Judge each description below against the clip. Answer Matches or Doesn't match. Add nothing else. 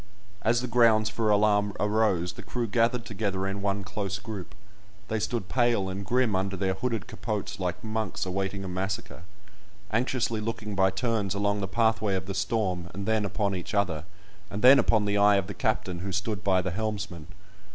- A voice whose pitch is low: Matches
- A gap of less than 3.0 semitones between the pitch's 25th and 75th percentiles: Matches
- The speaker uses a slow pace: Doesn't match